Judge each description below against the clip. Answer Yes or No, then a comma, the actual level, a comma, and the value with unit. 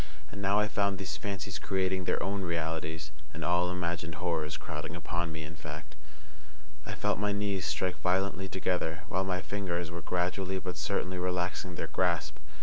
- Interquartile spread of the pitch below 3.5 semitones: Yes, narrow, 2.4 semitones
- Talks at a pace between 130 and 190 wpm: Yes, average, 170 wpm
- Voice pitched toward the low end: Yes, very low, 90 Hz